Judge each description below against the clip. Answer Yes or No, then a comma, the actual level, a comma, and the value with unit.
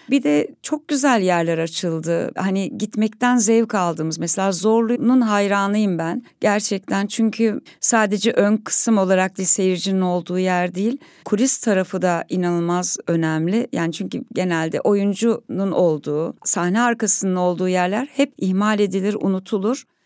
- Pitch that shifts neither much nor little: Yes, average, 4.0 semitones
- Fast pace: No, average, 130 wpm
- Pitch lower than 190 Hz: No, high, 195 Hz